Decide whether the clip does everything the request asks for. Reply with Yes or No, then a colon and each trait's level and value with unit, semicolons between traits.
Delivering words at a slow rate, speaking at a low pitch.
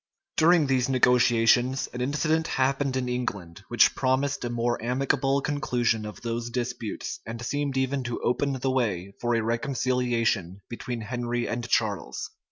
No: average, 155 wpm; low, 125 Hz